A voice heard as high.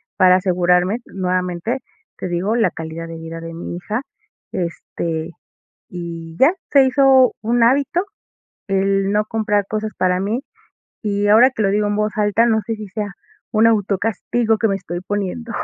Yes: high, 205 Hz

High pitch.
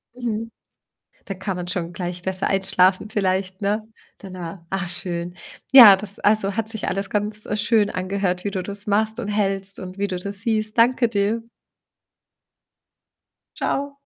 Yes: high, 200 Hz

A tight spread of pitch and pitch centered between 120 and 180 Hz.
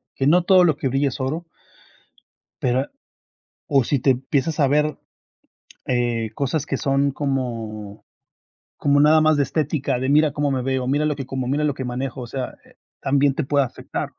Yes: narrow, 2.3 semitones; low, 135 Hz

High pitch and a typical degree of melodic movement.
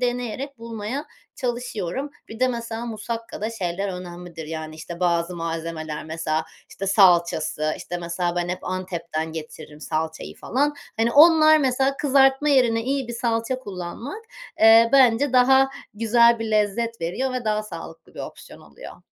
No: high, 220 Hz; wide, 6.5 semitones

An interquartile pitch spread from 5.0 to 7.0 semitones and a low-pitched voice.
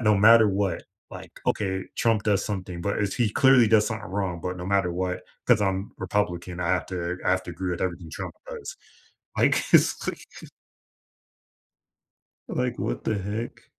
No: average, 2.7 semitones; very low, 95 Hz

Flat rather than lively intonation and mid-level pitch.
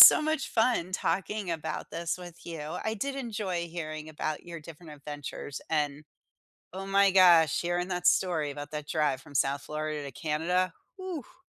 No: average, 4.0 semitones; medium, 170 Hz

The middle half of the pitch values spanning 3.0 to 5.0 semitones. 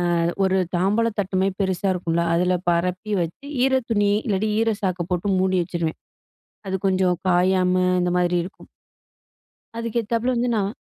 No: narrow, 2.5 semitones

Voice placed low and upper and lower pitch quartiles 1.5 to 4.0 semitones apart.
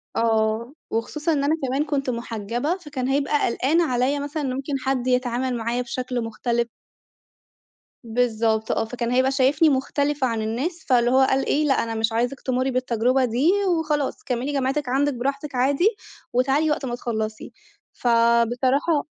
No: very high, 255 Hz; average, 3.1 semitones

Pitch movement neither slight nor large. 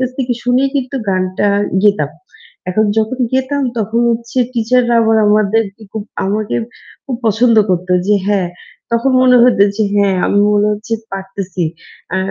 Yes: average, 3.7 semitones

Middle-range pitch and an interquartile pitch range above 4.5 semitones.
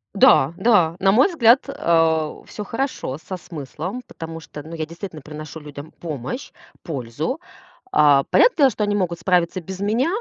Yes: medium, 170 Hz; average, 5.3 semitones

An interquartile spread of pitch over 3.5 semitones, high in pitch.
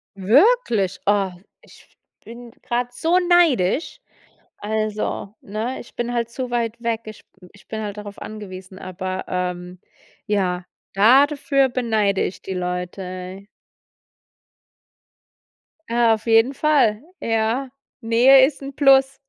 Yes: average, 4.7 semitones; high, 220 Hz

